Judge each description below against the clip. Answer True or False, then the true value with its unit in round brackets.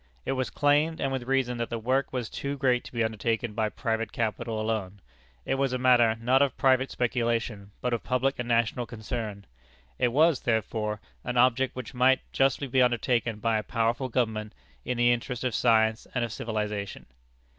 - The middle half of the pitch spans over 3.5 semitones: False (2.5 semitones)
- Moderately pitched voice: False (120 Hz)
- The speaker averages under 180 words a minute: False (190 wpm)